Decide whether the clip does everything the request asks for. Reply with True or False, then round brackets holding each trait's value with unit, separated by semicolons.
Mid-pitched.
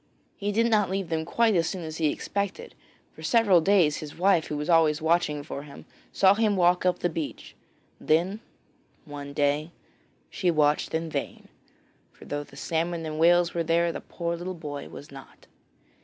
True (165 Hz)